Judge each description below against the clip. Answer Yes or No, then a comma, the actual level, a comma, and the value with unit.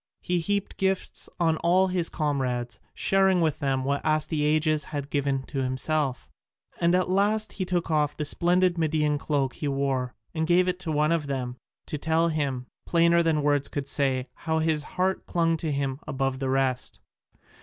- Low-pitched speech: No, medium, 155 Hz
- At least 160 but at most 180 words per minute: Yes, average, 175 wpm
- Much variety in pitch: No, average, 3.7 semitones